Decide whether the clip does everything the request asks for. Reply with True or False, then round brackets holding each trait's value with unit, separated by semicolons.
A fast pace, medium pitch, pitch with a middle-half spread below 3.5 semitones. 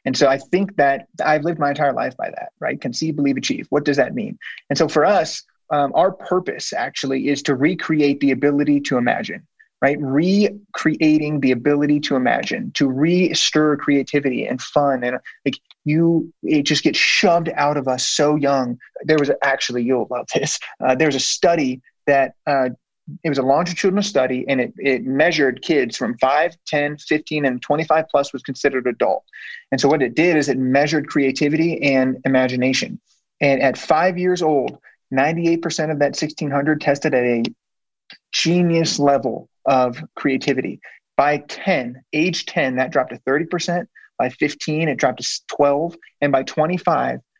False (170 wpm; 145 Hz; 2.9 semitones)